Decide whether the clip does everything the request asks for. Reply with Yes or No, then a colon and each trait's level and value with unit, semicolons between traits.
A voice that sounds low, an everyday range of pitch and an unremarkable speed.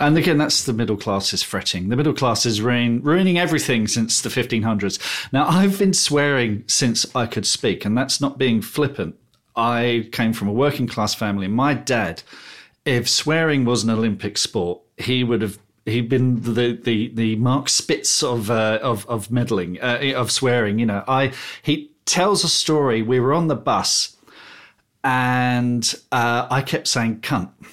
Yes: low, 120 Hz; average, 3.4 semitones; average, 175 wpm